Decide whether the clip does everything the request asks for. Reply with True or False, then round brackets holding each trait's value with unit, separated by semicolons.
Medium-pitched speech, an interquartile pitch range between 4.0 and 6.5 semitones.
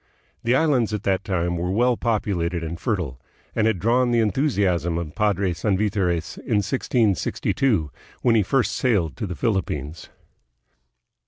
False (100 Hz; 4.9 semitones)